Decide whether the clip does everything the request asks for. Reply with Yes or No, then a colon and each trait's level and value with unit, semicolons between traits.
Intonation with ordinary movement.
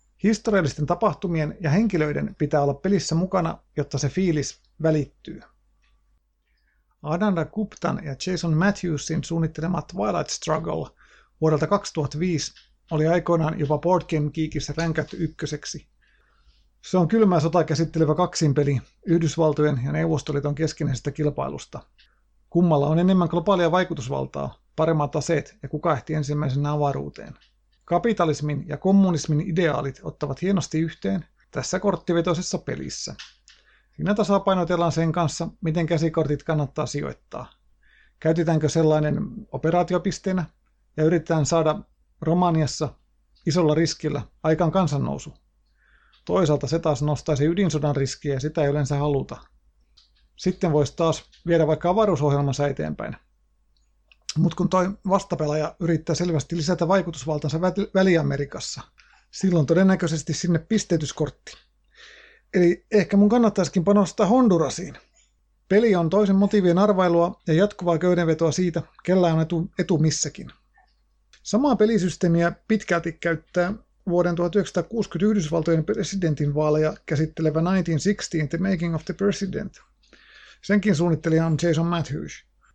Yes: average, 3.3 semitones